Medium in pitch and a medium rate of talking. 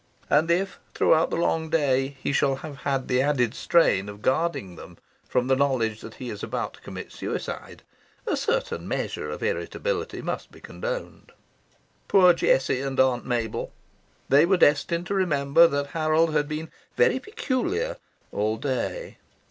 Yes: medium, 145 Hz; average, 160 wpm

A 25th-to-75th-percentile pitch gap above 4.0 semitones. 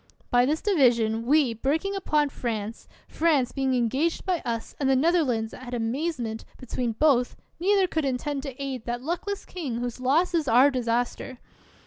Yes: average, 4.6 semitones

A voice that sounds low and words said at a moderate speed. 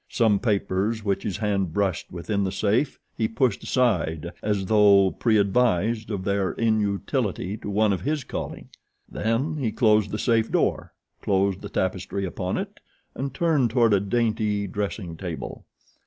Yes: low, 105 Hz; average, 155 wpm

